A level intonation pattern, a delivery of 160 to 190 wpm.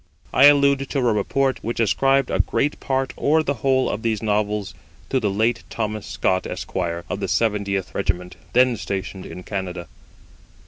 No: average, 5.2 semitones; average, 170 wpm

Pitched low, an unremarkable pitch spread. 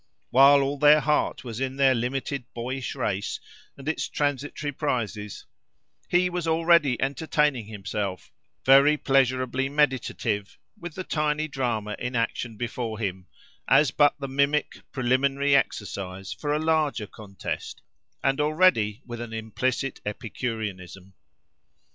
Yes: low, 130 Hz; average, 4.7 semitones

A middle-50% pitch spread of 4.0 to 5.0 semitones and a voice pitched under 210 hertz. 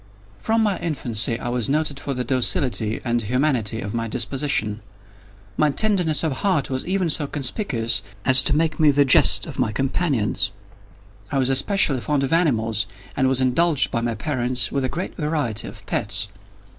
Yes: average, 4.6 semitones; low, 135 Hz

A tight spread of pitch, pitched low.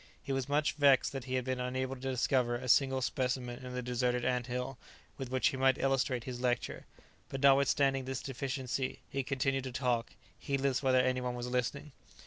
Yes: narrow, 1.3 semitones; low, 130 Hz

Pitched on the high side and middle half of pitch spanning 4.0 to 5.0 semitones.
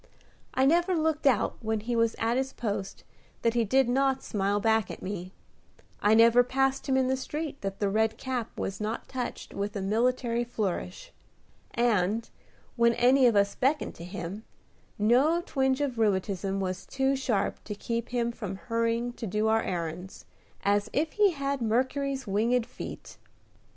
Yes: high, 230 Hz; average, 4.3 semitones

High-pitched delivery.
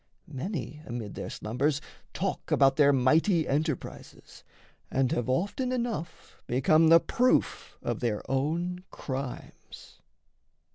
No: medium, 145 Hz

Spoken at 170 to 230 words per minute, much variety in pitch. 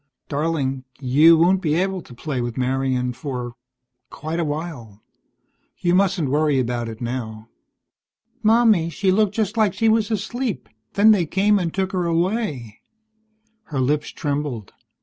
No: average, 150 wpm; wide, 6.8 semitones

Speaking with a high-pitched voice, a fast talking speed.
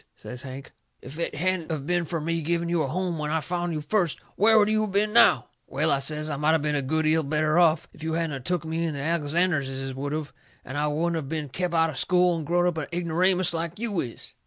No: medium, 160 Hz; fast, 270 wpm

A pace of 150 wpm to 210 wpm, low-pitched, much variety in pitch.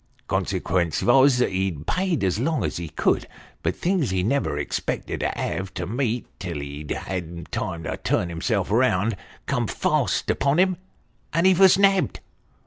Yes: average, 165 wpm; low, 105 Hz; wide, 8.7 semitones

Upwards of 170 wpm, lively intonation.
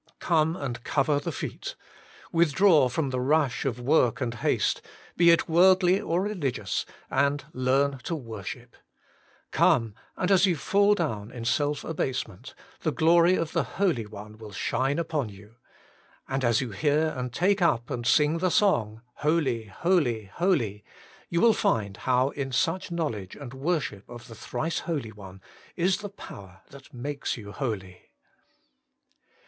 No: average, 155 wpm; wide, 6.4 semitones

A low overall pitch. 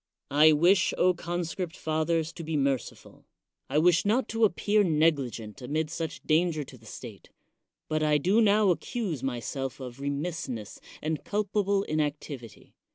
No: medium, 155 Hz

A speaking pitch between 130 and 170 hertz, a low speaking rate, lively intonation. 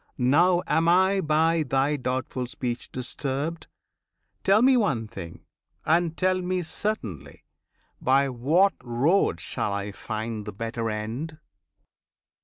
Yes: medium, 140 Hz; slow, 120 wpm; wide, 6.9 semitones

